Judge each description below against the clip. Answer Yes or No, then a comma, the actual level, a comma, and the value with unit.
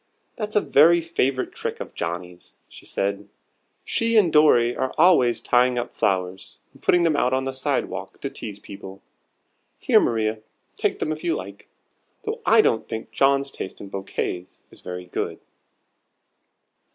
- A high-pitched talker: No, low, 120 Hz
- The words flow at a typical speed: Yes, average, 160 wpm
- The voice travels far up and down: Yes, wide, 7.7 semitones